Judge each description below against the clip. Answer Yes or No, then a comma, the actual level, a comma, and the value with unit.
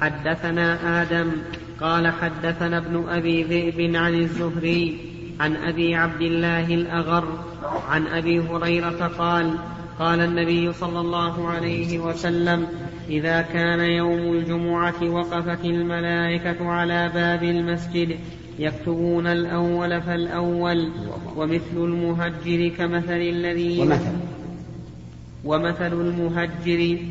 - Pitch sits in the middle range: Yes, medium, 170 Hz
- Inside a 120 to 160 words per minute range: No, average, 95 wpm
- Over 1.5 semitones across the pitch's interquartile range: No, narrow, 0.5 semitones